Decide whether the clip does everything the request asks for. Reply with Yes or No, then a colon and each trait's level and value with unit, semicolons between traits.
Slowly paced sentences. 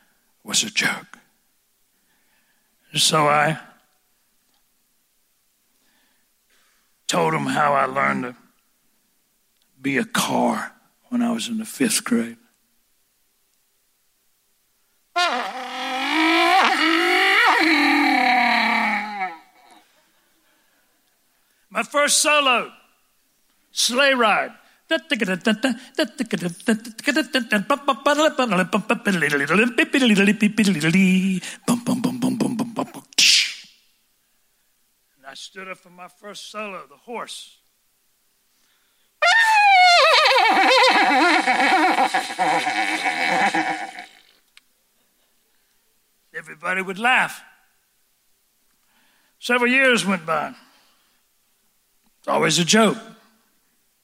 Yes: slow, 50 wpm